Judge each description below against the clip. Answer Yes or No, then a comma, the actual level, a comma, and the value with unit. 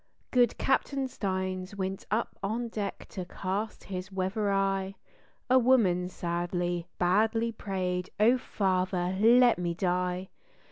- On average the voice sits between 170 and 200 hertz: Yes, high, 190 Hz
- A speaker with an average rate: No, slow, 125 wpm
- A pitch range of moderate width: Yes, average, 3.4 semitones